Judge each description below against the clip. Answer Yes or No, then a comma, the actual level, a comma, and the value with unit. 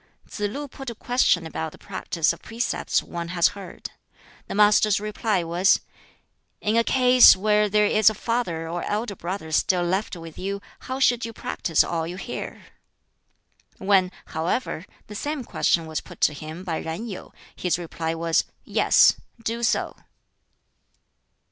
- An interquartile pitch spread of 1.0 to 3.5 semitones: No, average, 4.6 semitones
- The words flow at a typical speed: Yes, average, 160 wpm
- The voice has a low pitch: No, high, 195 Hz